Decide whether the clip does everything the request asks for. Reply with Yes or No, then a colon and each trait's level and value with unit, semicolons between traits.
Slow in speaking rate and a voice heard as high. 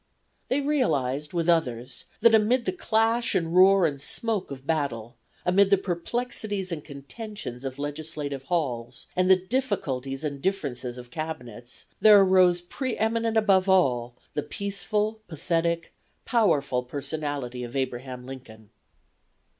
No: slow, 130 wpm; medium, 165 Hz